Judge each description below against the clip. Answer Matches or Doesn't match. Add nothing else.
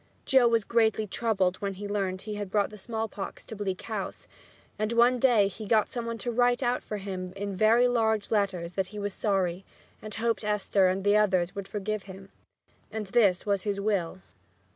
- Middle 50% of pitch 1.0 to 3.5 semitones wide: Matches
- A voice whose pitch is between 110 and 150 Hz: Doesn't match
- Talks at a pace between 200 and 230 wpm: Matches